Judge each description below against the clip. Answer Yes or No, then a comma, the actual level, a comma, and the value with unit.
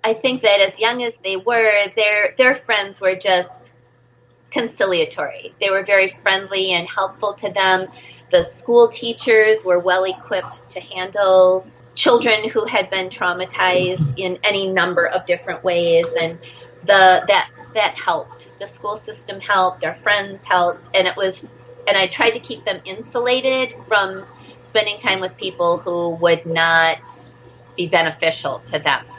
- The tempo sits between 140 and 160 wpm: Yes, average, 155 wpm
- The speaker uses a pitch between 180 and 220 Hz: Yes, high, 190 Hz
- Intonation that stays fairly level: No, average, 3.3 semitones